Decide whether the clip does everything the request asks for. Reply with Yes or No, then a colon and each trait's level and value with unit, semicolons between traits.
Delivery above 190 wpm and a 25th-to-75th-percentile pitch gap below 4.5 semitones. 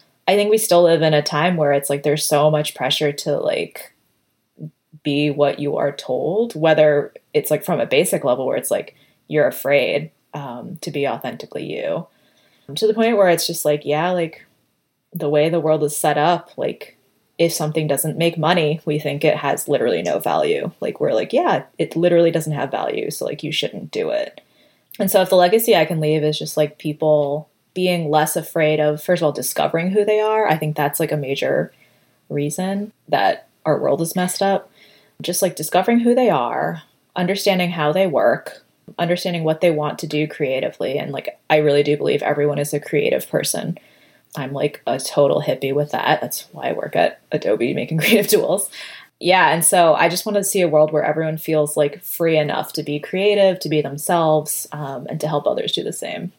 Yes: fast, 205 wpm; average, 3.4 semitones